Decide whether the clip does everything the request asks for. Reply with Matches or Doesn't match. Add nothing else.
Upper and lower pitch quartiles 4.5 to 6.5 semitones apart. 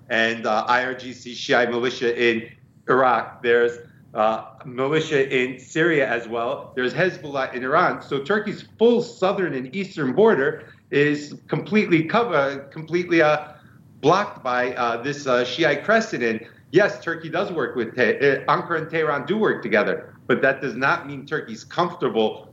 Matches